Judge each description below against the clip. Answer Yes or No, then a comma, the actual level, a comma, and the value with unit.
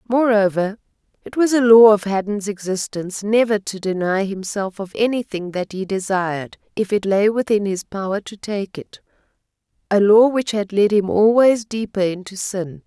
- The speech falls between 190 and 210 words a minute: No, average, 165 wpm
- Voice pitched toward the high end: Yes, high, 205 Hz